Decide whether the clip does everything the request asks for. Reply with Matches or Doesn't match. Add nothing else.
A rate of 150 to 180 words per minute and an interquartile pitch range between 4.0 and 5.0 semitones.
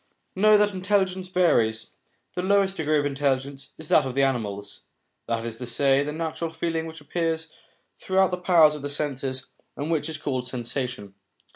Matches